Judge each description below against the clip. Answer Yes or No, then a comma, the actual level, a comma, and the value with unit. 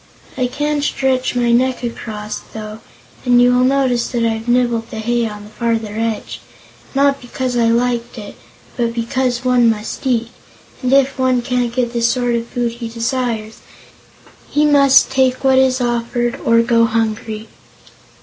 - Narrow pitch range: Yes, narrow, 1.8 semitones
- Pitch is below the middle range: No, high, 240 Hz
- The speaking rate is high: No, average, 165 wpm